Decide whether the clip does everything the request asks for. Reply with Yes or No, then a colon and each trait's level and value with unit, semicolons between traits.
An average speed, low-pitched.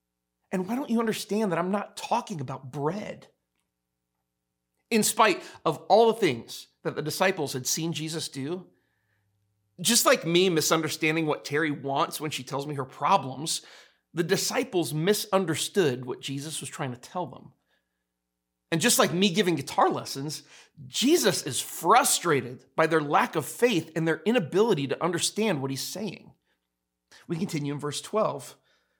No: average, 155 wpm; medium, 155 Hz